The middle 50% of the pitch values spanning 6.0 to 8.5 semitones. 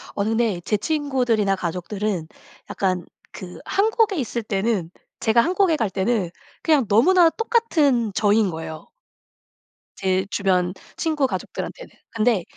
Yes: wide, 7.3 semitones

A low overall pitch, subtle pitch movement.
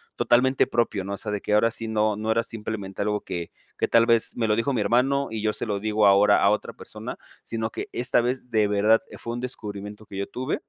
Yes: low, 110 Hz; narrow, 2.2 semitones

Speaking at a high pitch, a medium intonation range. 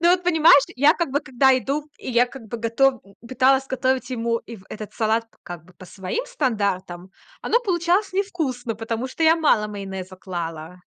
No: very high, 250 Hz; wide, 6.4 semitones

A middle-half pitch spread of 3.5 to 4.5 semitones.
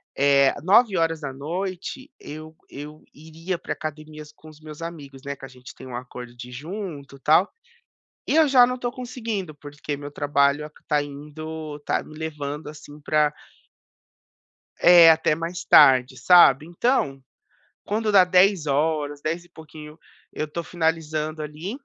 No: average, 3.1 semitones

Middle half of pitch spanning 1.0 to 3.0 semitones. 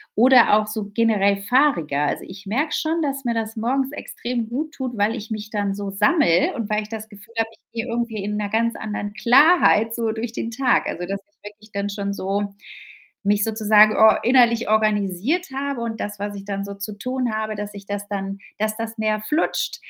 Yes: narrow, 2.6 semitones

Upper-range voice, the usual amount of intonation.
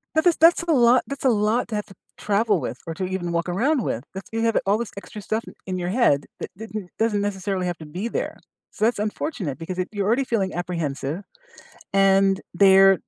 Yes: high, 200 Hz; average, 3.8 semitones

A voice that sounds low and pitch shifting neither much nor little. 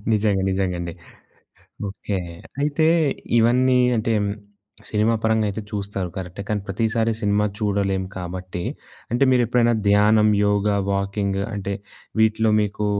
No: low, 105 Hz; narrow, 2.2 semitones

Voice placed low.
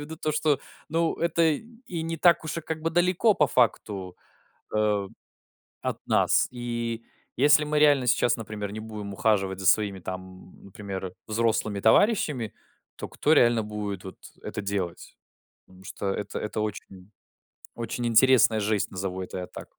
Yes: low, 110 Hz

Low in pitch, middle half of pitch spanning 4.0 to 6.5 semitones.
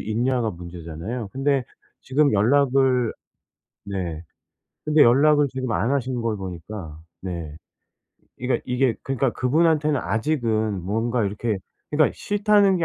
Yes: low, 125 Hz; wide, 5.5 semitones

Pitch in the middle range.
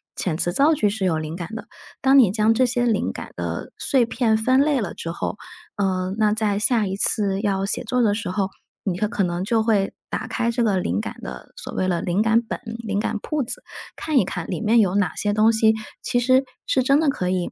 No: high, 215 Hz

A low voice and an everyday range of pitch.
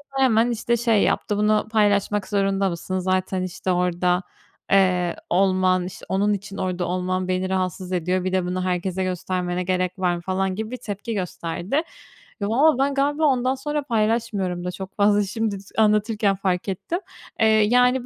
No: high, 195 Hz; average, 3.0 semitones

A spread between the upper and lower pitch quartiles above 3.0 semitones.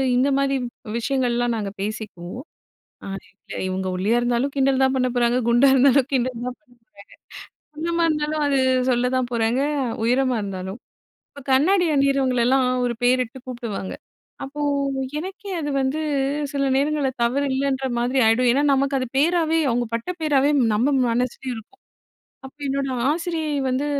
No: average, 2.7 semitones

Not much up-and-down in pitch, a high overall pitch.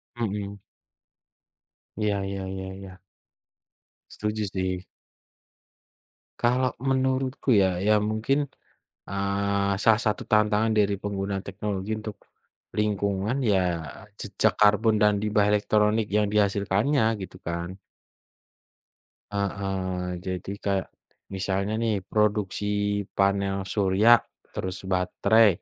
No: narrow, 1.8 semitones; low, 100 Hz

